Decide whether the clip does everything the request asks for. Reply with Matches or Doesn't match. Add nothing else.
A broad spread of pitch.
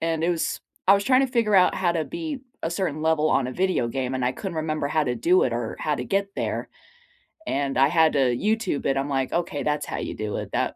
Matches